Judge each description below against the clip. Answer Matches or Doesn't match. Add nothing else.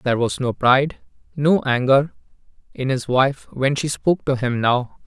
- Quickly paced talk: Doesn't match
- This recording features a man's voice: Matches